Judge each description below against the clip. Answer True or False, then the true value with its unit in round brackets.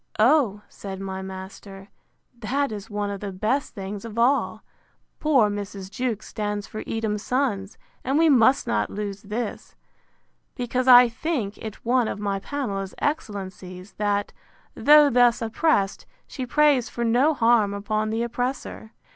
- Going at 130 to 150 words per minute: True (145 wpm)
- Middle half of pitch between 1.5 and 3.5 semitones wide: False (3.9 semitones)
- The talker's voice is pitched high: True (215 Hz)